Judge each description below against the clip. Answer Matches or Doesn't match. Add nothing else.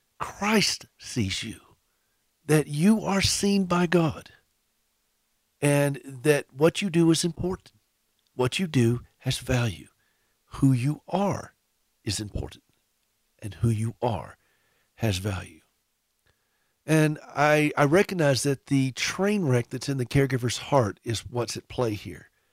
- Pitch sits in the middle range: Doesn't match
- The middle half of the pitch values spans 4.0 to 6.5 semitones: Matches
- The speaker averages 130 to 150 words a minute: Matches